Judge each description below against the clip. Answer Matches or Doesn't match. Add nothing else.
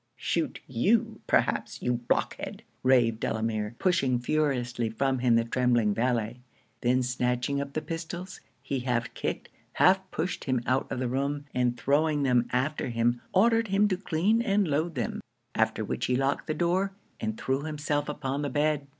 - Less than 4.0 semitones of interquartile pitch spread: Doesn't match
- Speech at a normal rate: Matches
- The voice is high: Doesn't match